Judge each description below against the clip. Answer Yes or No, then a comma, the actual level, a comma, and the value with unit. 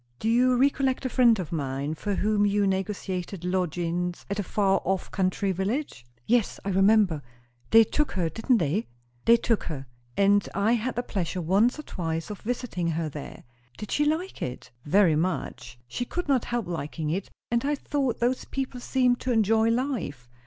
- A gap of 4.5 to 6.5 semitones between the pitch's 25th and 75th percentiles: Yes, wide, 5.6 semitones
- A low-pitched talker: No, high, 205 Hz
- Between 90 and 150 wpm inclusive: No, average, 180 wpm